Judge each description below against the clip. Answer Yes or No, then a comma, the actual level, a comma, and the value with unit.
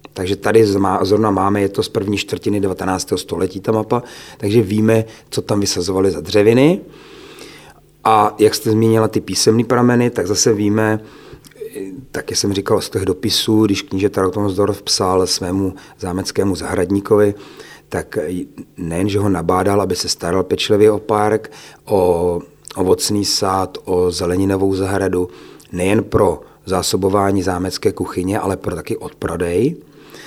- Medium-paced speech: Yes, average, 140 wpm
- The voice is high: No, low, 100 Hz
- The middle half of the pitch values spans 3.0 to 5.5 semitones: No, narrow, 2.4 semitones